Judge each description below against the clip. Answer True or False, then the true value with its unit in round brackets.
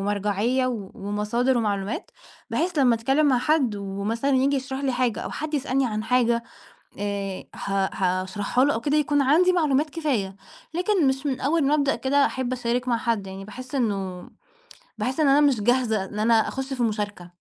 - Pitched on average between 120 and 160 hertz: False (245 Hz)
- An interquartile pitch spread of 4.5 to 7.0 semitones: True (4.9 semitones)